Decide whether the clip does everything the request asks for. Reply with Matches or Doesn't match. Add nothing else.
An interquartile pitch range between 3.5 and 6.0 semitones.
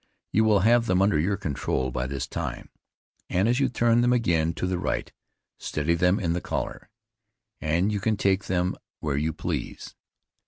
Matches